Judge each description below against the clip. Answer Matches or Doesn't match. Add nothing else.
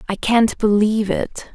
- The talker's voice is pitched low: Doesn't match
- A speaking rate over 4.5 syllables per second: Doesn't match